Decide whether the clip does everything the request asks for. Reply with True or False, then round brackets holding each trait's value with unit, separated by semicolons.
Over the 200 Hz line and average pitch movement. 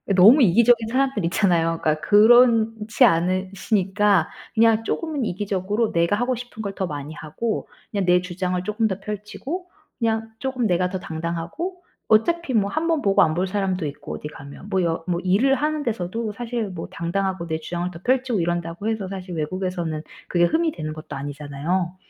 False (195 Hz; 4.9 semitones)